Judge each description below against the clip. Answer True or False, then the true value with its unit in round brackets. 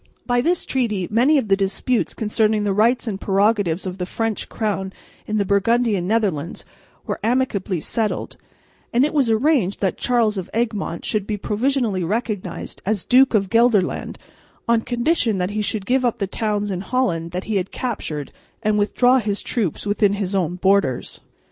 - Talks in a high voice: True (210 Hz)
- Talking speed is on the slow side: False (175 wpm)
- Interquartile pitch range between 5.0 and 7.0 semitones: False (3.6 semitones)